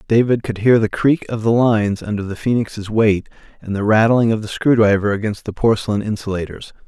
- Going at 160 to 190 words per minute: No, average, 200 wpm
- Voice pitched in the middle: No, low, 110 Hz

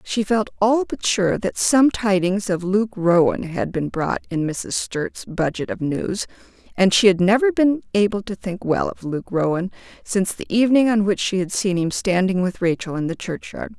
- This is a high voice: Yes, high, 195 Hz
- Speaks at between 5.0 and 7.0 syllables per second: No, 4.7 syllables/s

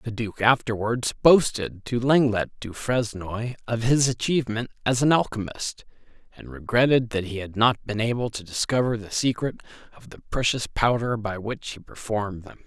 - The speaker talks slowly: No, average, 165 wpm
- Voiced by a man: Yes, male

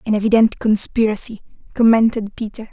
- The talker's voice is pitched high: Yes, high, 220 Hz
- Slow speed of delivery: Yes, slow, 110 wpm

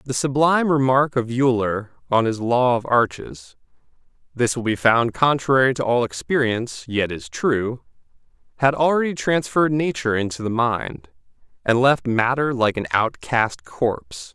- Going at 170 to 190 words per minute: No, average, 145 wpm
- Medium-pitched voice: No, low, 120 Hz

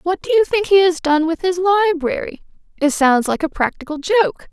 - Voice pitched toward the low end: No, very high, 335 Hz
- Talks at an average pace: No, fast, 225 wpm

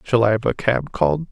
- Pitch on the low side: Yes, low, 115 Hz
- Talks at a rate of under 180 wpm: No, fast, 275 wpm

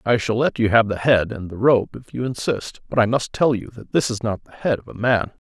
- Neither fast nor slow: No, fast, 295 wpm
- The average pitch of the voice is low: Yes, low, 115 Hz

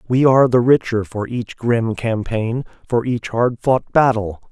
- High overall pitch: No, low, 115 Hz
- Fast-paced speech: No, average, 175 wpm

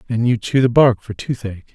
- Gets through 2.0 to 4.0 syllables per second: No, 6.0 syllables/s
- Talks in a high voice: No, low, 120 Hz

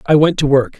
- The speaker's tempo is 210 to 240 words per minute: No, fast, 305 wpm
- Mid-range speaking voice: Yes, medium, 145 Hz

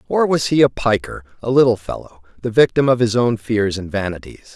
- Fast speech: Yes, fast, 210 wpm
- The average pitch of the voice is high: No, low, 120 Hz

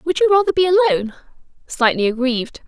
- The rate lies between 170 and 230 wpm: No, average, 155 wpm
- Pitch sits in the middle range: No, very high, 300 Hz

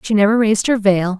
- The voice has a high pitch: Yes, high, 210 Hz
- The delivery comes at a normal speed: No, fast, 250 wpm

